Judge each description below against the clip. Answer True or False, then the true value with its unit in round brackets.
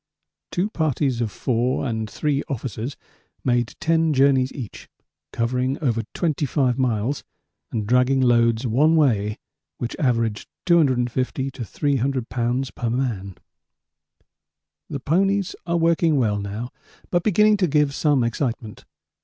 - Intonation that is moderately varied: True (4.1 semitones)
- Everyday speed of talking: False (125 wpm)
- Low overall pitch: True (130 Hz)